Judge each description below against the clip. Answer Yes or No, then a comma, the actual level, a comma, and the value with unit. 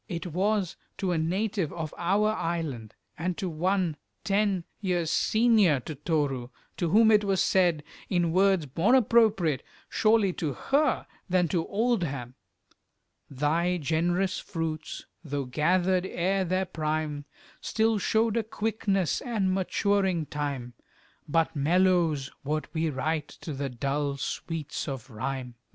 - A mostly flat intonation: No, average, 4.6 semitones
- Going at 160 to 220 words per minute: No, slow, 135 wpm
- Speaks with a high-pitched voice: No, medium, 175 Hz